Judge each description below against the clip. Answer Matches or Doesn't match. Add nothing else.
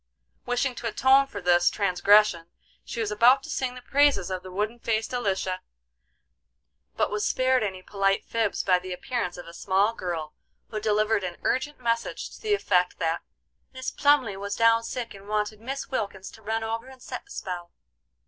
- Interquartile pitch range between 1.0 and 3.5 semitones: Doesn't match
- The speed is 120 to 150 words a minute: Doesn't match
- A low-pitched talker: Doesn't match